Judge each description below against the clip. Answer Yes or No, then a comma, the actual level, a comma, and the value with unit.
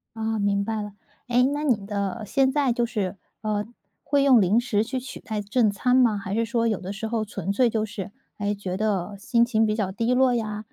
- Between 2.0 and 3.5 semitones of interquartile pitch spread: Yes, average, 2.9 semitones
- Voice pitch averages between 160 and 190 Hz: No, high, 220 Hz